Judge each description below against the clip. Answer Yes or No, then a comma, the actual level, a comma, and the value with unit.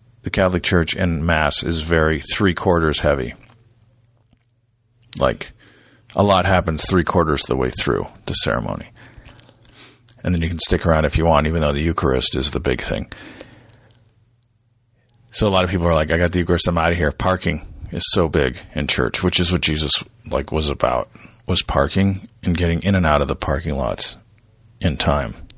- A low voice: Yes, very low, 90 Hz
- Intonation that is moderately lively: No, wide, 5.9 semitones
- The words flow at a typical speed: Yes, average, 190 wpm